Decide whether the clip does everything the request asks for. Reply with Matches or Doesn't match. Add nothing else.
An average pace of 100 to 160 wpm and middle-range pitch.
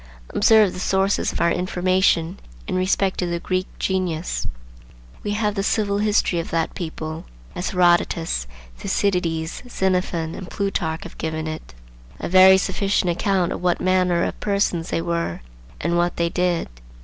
Matches